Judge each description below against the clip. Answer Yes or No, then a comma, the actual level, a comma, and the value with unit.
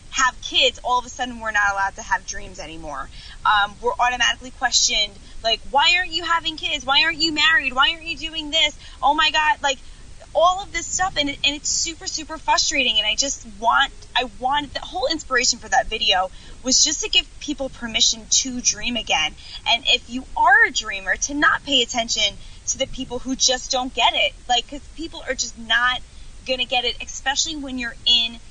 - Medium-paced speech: No, fast, 210 wpm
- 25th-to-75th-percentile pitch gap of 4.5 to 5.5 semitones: Yes, average, 4.8 semitones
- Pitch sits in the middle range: No, very high, 265 Hz